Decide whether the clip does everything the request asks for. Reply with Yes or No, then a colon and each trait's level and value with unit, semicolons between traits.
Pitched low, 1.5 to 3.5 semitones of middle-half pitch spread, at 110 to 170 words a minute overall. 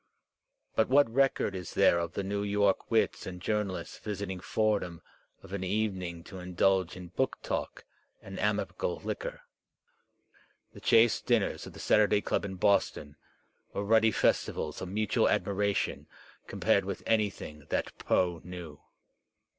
Yes: low, 100 Hz; average, 3.0 semitones; average, 145 wpm